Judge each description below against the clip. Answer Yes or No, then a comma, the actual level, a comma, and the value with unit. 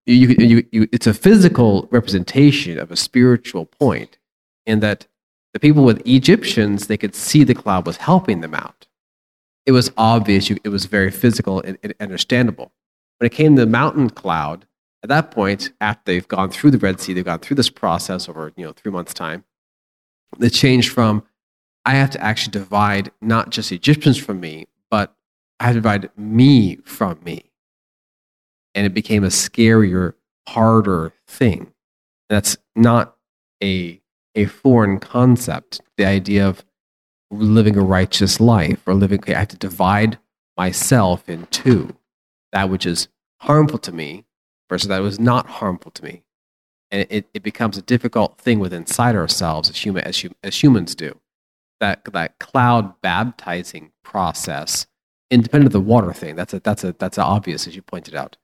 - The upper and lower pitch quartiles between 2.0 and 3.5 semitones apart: No, average, 4.4 semitones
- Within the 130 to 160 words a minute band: No, average, 170 wpm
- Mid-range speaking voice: No, low, 105 Hz